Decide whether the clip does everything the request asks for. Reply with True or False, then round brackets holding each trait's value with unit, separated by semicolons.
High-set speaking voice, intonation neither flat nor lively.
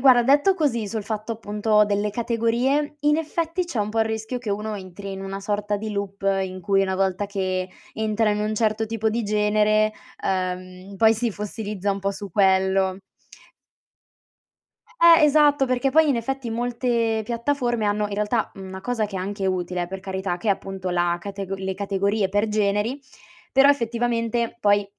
True (210 Hz; 3.2 semitones)